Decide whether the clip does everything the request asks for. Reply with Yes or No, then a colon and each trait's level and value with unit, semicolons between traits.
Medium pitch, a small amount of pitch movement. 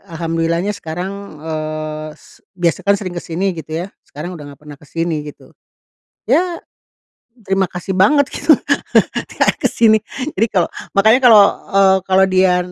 No: medium, 180 Hz; average, 3.5 semitones